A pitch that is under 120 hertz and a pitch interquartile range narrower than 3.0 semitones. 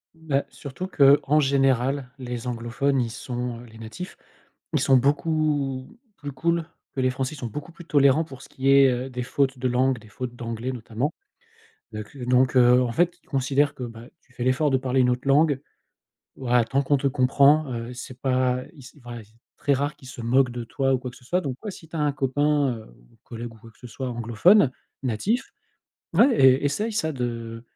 No: low, 130 Hz; narrow, 2.6 semitones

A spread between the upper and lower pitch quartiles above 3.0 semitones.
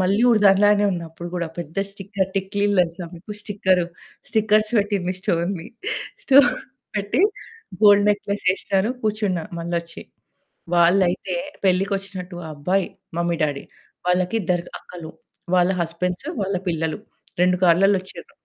No: narrow, 2.6 semitones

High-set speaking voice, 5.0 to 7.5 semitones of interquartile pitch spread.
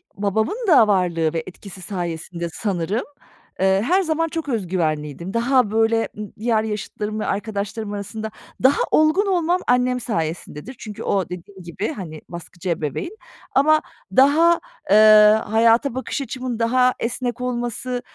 Yes: high, 220 Hz; average, 5.3 semitones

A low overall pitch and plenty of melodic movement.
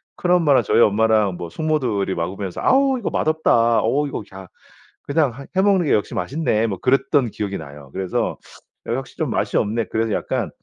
Yes: low, 115 Hz; wide, 7.0 semitones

